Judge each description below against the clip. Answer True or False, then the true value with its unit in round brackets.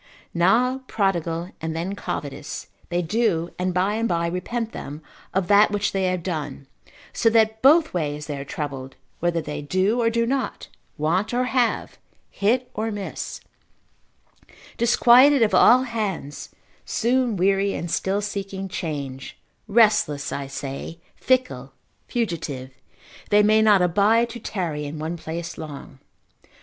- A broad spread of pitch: True (5.9 semitones)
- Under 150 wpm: True (140 wpm)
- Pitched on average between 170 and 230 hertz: True (190 Hz)